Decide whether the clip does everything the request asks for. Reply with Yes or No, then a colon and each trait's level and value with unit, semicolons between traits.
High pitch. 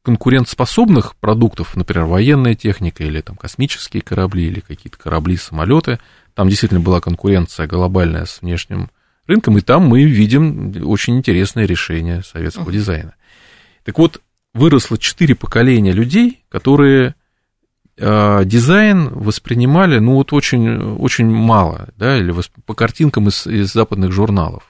No: low, 105 Hz